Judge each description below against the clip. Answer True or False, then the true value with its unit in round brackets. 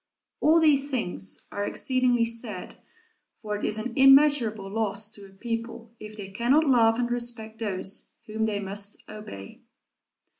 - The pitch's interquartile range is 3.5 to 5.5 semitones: False (3.1 semitones)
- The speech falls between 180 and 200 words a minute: False (150 wpm)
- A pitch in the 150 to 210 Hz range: False (225 Hz)